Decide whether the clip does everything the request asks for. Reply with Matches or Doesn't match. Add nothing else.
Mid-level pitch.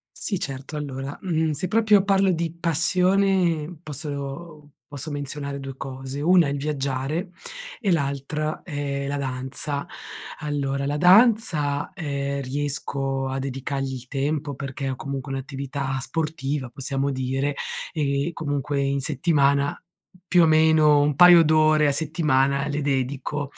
Matches